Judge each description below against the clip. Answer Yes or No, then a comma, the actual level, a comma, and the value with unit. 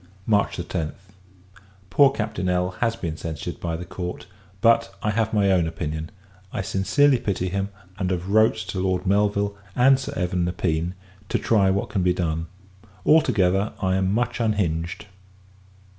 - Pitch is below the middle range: Yes, very low, 95 Hz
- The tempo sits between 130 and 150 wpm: No, average, 160 wpm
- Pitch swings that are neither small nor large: Yes, average, 3.3 semitones